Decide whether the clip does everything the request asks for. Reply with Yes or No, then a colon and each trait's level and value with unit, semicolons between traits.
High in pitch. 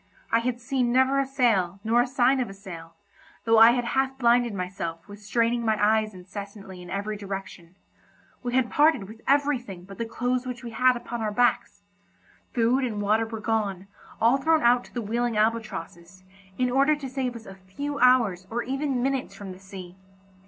Yes: high, 230 Hz